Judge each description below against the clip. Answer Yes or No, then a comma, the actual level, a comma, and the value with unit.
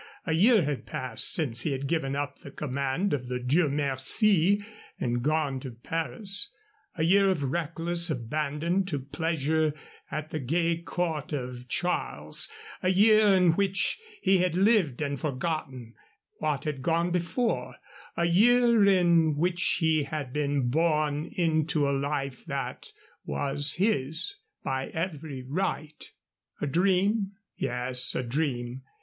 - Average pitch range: Yes, average, 4.3 semitones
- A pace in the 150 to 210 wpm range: No, average, 140 wpm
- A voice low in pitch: No, medium, 155 Hz